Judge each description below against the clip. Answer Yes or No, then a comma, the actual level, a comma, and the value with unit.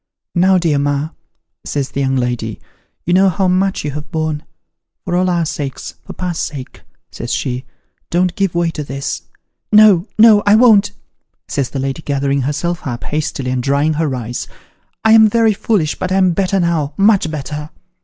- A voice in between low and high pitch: Yes, medium, 160 Hz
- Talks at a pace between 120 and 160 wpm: No, average, 195 wpm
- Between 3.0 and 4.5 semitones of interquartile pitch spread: No, average, 5.1 semitones